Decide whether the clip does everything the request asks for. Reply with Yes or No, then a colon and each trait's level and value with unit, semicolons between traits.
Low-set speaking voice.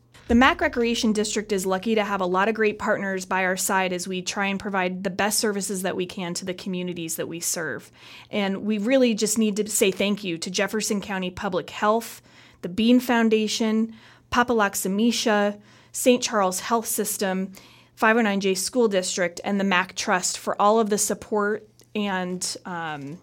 No: high, 200 Hz